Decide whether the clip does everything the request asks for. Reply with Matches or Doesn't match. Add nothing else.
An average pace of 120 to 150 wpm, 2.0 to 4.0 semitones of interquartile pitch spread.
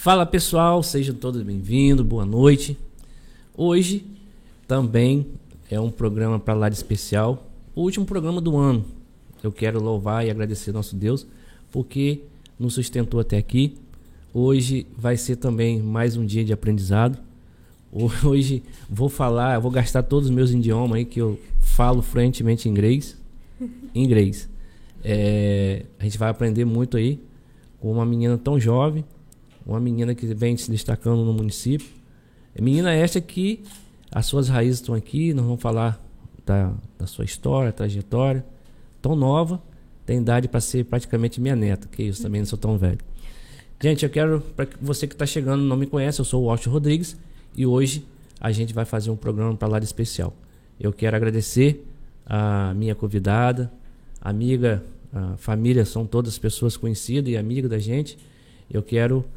Doesn't match